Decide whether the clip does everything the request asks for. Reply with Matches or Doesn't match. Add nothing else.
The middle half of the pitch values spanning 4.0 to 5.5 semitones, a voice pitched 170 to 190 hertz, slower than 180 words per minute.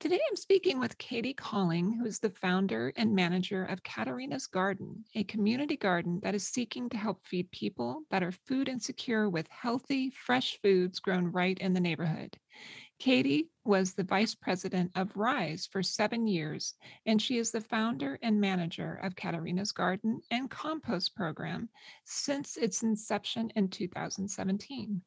Doesn't match